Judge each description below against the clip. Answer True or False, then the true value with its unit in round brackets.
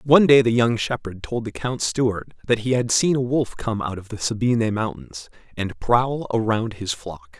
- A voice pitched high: False (115 Hz)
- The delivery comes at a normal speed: False (210 wpm)